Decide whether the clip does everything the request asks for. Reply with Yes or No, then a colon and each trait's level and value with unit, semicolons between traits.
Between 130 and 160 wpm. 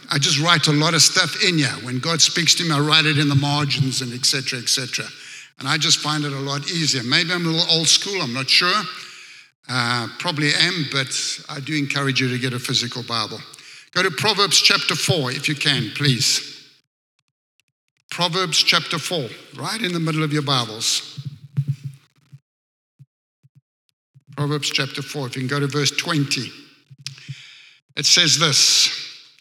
No: average, 180 wpm